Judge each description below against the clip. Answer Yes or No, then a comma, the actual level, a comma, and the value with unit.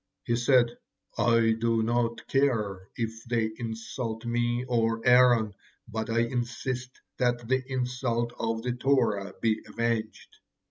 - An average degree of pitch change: No, narrow, 1.5 semitones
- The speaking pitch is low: Yes, low, 120 Hz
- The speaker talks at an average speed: No, slow, 130 wpm